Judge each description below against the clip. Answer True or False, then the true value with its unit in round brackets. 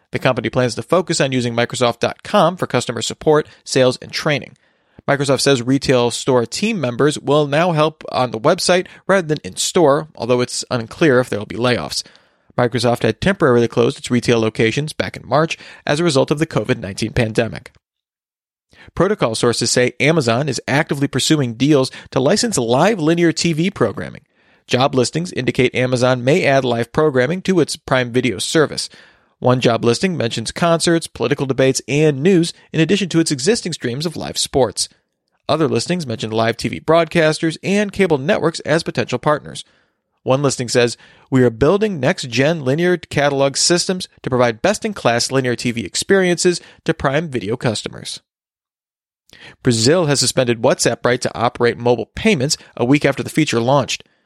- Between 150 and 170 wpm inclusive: True (165 wpm)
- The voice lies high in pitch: False (140 Hz)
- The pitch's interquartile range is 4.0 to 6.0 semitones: True (5.1 semitones)